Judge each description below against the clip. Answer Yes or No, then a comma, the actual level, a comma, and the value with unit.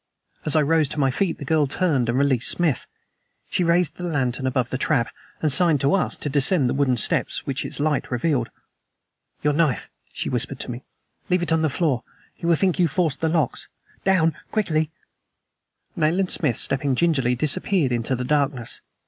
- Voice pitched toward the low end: No, medium, 145 Hz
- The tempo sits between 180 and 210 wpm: Yes, average, 190 wpm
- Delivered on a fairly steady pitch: No, average, 4.2 semitones